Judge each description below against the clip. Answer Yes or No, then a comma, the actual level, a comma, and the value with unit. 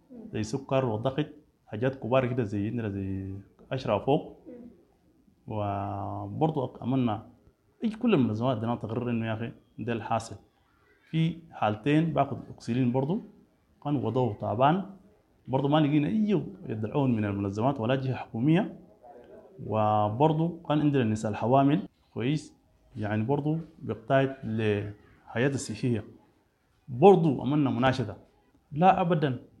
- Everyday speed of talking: No, slow, 115 wpm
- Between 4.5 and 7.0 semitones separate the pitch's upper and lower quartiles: Yes, average, 5.3 semitones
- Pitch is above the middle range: No, low, 130 Hz